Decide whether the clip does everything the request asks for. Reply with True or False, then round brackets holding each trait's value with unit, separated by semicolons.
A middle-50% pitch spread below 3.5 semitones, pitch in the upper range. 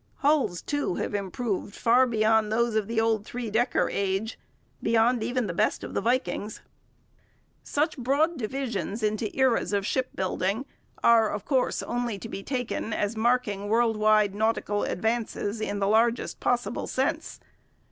True (2.9 semitones; 225 Hz)